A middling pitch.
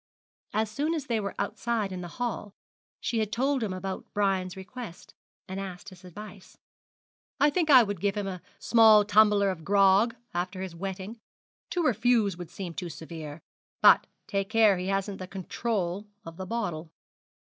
No: high, 200 Hz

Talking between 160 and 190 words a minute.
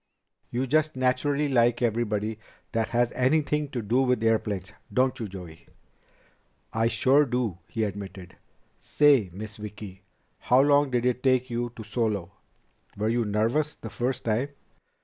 No: average, 150 wpm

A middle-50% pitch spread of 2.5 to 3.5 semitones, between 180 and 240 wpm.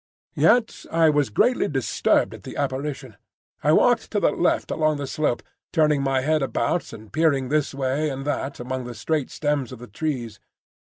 Yes: average, 2.9 semitones; average, 185 wpm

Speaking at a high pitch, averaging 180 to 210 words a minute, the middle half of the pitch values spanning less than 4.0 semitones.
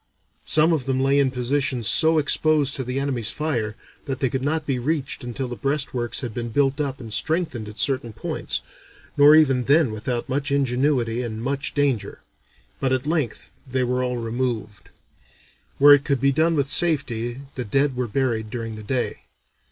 No: low, 130 Hz; average, 185 wpm; average, 3.0 semitones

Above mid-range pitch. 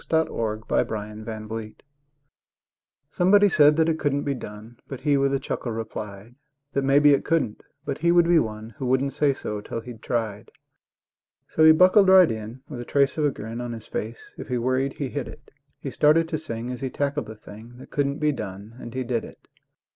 No: low, 130 Hz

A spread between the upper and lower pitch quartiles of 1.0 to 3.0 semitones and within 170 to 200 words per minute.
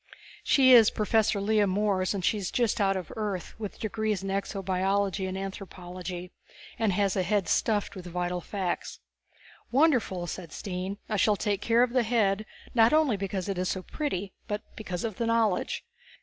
Yes: average, 2.7 semitones; average, 175 wpm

